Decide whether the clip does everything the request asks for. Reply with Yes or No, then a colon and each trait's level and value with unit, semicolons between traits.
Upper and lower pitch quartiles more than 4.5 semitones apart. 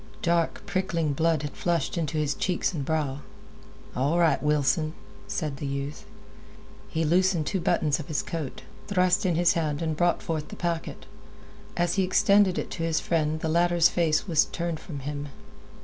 No: narrow, 2.5 semitones